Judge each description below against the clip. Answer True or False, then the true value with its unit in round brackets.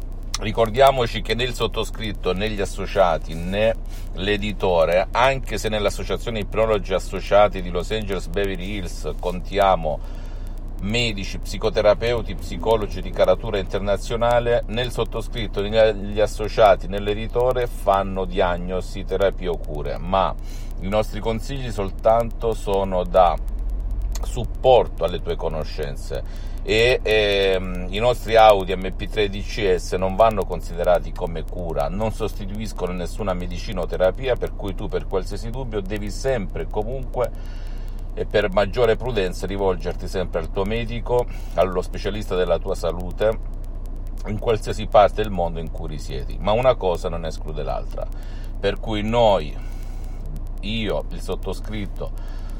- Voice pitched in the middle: False (100 Hz)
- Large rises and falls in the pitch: False (3.1 semitones)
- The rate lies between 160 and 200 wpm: False (120 wpm)